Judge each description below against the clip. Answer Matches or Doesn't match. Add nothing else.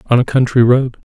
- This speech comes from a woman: Doesn't match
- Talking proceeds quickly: Matches